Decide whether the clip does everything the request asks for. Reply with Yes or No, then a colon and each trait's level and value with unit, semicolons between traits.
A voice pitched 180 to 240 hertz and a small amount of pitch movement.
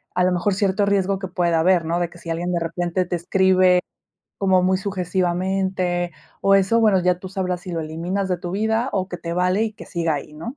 Yes: medium, 185 Hz; narrow, 1.7 semitones